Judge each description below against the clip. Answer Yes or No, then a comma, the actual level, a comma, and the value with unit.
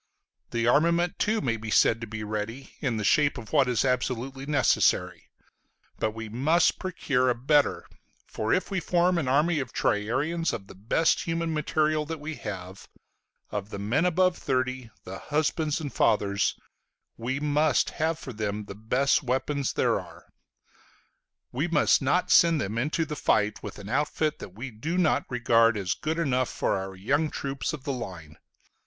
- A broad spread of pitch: Yes, wide, 5.8 semitones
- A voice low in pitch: Yes, low, 130 Hz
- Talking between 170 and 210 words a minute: Yes, average, 175 wpm